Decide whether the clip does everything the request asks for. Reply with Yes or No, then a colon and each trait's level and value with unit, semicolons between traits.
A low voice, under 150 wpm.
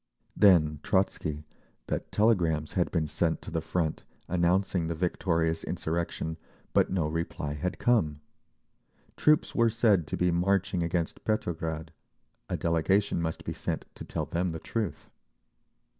Yes: very low, 85 Hz; slow, 135 wpm